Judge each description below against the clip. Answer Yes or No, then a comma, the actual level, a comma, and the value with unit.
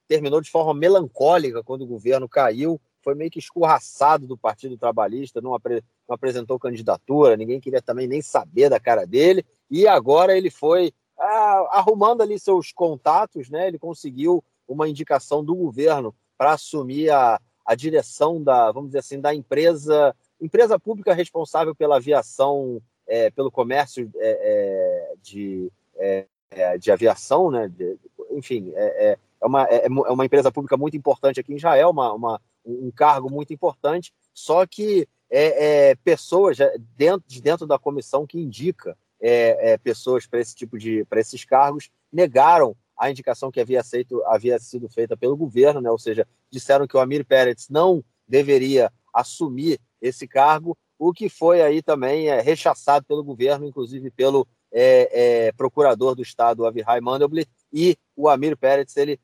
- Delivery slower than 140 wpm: No, average, 165 wpm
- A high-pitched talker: No, medium, 150 Hz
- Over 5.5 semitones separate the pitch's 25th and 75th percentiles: Yes, wide, 6.1 semitones